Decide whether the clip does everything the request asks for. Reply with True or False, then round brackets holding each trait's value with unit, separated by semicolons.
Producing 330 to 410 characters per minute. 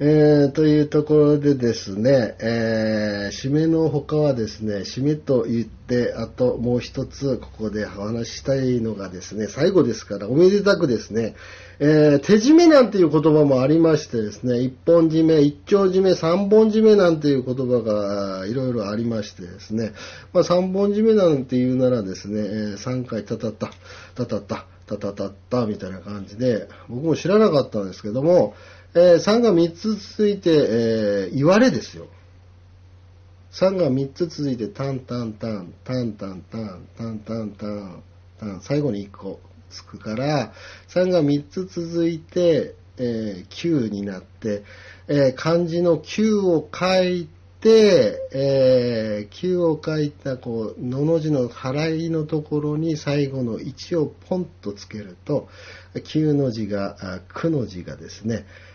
False (270 characters per minute)